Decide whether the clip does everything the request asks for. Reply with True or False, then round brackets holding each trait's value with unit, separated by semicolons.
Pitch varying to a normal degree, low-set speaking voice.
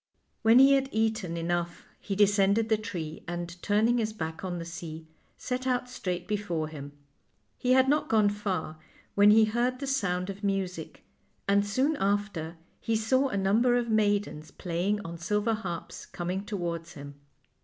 False (4.3 semitones; 205 Hz)